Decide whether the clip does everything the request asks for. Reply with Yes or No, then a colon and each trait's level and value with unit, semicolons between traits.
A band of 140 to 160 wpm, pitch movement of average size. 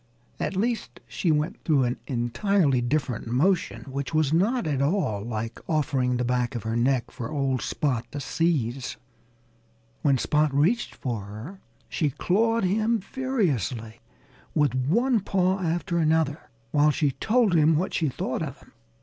No: average, 155 wpm; wide, 6.5 semitones